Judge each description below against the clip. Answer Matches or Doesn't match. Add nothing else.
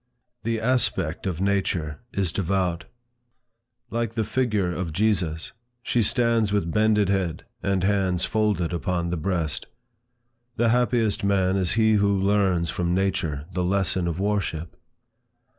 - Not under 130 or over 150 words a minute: Matches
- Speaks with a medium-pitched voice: Doesn't match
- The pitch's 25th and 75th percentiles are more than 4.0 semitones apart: Doesn't match